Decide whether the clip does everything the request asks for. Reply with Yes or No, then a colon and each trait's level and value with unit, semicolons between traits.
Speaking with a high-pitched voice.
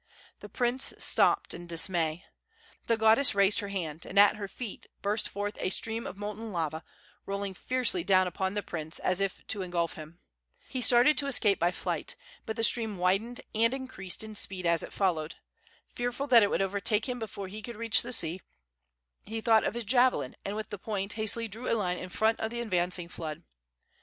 Yes: high, 205 Hz